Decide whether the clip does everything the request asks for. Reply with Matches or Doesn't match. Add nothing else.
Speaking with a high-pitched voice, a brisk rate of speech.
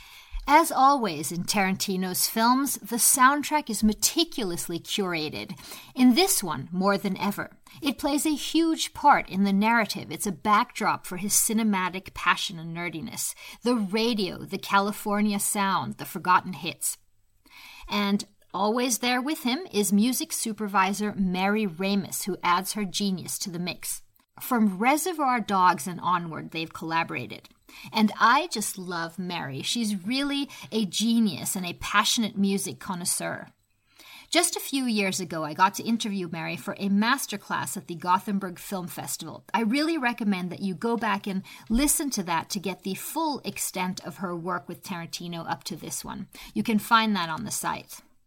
Doesn't match